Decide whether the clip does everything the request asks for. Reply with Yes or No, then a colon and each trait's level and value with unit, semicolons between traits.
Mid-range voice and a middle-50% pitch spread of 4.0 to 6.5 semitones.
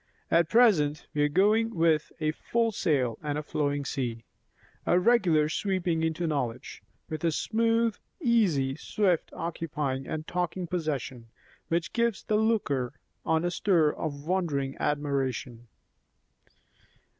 Yes: medium, 160 Hz; average, 4.8 semitones